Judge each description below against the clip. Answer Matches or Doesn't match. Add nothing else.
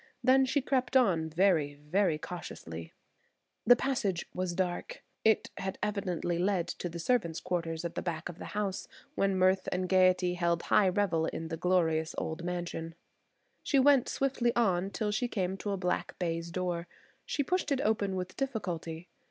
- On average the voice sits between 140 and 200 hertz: Matches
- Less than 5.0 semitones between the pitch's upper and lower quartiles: Matches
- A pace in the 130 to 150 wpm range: Doesn't match